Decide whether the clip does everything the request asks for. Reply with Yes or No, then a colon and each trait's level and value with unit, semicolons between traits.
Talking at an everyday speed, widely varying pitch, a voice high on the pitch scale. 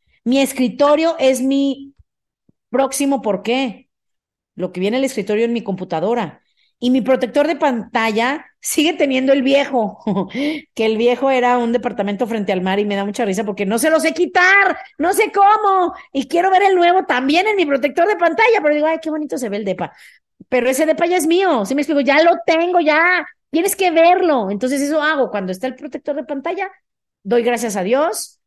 No: fast, 205 wpm; wide, 5.9 semitones; very high, 275 Hz